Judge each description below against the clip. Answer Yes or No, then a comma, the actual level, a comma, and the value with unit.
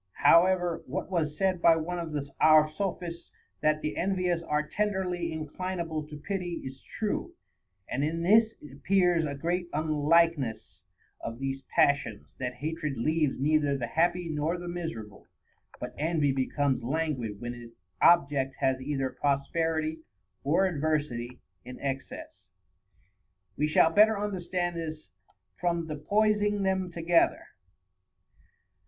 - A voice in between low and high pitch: Yes, medium, 160 Hz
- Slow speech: Yes, slow, 130 wpm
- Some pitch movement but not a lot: Yes, average, 3.7 semitones